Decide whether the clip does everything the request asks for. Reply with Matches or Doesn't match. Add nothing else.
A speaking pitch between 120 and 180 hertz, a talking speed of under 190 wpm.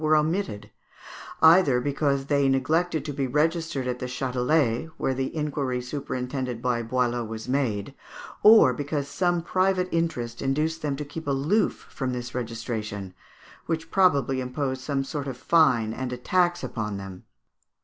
Matches